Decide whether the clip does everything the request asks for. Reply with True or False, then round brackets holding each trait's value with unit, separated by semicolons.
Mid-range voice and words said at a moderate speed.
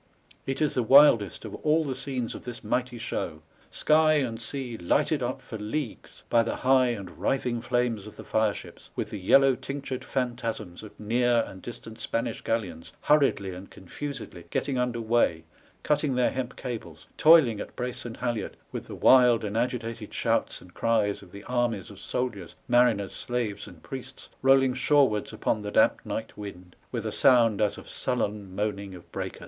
False (120 Hz; 180 wpm)